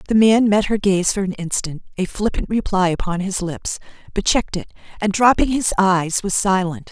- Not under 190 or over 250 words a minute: Yes, average, 200 wpm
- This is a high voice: Yes, high, 195 Hz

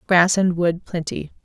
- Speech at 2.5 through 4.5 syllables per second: Yes, 4.2 syllables/s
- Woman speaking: Yes, female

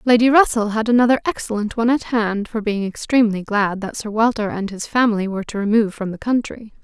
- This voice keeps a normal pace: No, fast, 210 wpm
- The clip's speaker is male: No, female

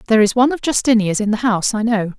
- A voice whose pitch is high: Yes, high, 225 Hz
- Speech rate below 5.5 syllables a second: No, 7.5 syllables/s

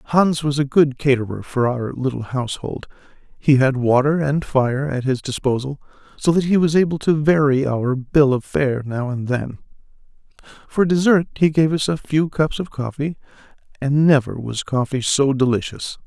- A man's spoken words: Yes, male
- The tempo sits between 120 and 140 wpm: No, average, 175 wpm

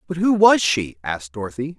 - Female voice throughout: No, male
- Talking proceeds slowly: No, average, 200 wpm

